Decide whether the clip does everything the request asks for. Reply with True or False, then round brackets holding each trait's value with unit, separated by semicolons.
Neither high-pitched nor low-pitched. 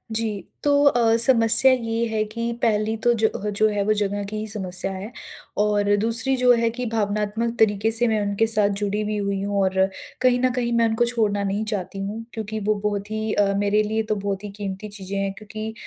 False (215 Hz)